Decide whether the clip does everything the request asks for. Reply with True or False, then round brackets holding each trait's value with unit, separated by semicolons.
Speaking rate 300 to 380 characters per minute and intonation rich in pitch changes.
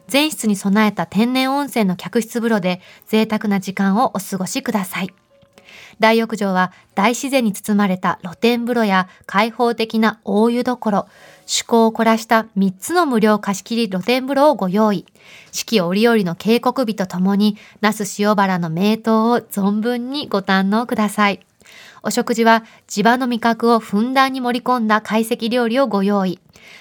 False (305 characters per minute; 2.9 semitones)